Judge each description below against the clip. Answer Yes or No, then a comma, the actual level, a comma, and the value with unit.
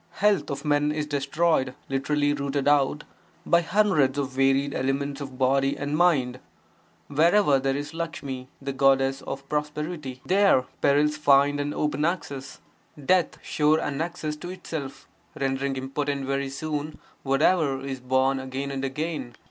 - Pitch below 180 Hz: Yes, medium, 140 Hz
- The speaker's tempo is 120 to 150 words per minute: Yes, average, 140 wpm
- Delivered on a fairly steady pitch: Yes, narrow, 2.1 semitones